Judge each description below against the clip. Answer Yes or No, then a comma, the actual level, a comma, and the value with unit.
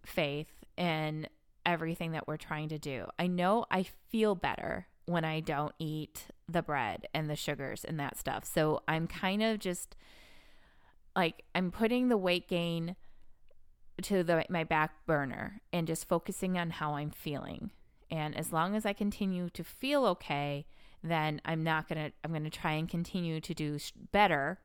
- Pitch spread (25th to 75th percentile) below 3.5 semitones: Yes, average, 2.8 semitones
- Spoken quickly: No, average, 175 wpm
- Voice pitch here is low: No, medium, 165 Hz